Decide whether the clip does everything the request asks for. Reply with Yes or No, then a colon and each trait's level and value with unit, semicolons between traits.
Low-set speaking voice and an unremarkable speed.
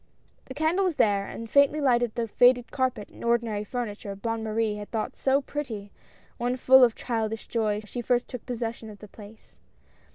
No: high, 230 Hz; average, 185 wpm